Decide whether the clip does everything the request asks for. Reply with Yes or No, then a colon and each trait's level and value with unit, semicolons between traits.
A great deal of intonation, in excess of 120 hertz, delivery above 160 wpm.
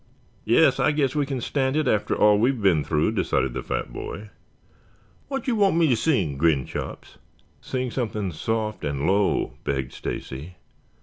No: wide, 8.7 semitones; low, 105 Hz; average, 170 wpm